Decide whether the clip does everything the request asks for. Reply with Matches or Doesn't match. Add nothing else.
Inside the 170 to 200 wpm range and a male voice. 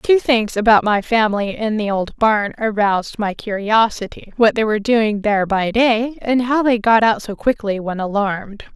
Doesn't match